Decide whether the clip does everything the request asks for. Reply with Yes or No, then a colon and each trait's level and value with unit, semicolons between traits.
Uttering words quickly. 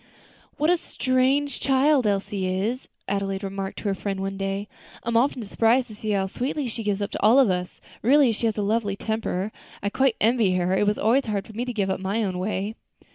Yes: fast, 230 wpm